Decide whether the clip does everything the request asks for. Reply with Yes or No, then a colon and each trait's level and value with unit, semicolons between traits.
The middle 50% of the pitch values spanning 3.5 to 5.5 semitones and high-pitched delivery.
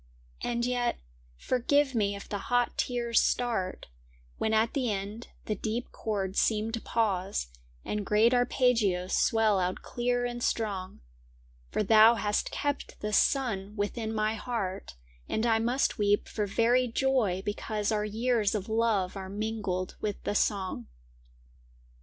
No: average, 2.9 semitones; high, 220 Hz